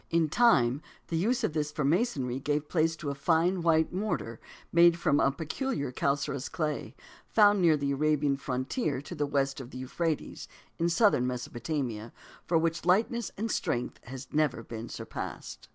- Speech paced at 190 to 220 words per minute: No, average, 170 wpm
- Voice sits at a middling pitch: Yes, medium, 150 Hz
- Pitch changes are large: No, average, 4.0 semitones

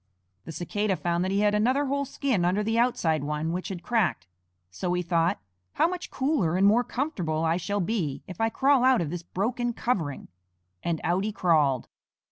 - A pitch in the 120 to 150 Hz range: No, high, 190 Hz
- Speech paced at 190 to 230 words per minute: Yes, average, 195 wpm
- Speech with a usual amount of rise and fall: No, wide, 6.0 semitones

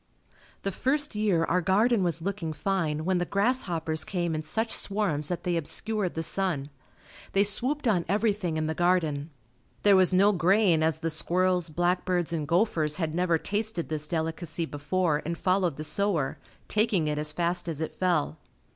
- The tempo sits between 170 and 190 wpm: Yes, average, 175 wpm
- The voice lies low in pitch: No, medium, 175 Hz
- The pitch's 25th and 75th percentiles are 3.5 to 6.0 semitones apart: Yes, average, 3.8 semitones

